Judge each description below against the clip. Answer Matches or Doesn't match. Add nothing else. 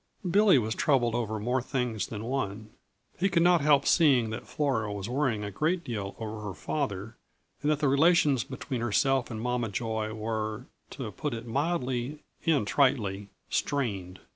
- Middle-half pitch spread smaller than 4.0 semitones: Doesn't match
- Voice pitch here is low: Matches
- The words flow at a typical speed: Matches